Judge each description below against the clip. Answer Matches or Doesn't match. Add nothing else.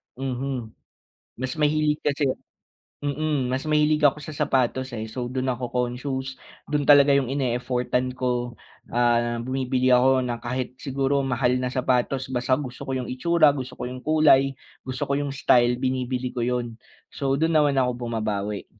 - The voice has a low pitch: Matches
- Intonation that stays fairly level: Matches